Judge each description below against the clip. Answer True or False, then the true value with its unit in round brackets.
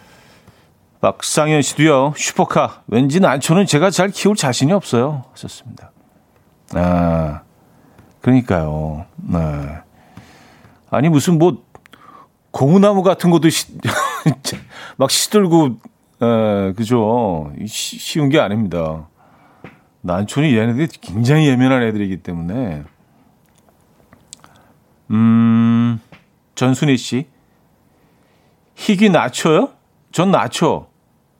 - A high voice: False (120 Hz)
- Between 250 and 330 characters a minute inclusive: False (190 characters per minute)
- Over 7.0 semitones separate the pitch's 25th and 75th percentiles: True (8.0 semitones)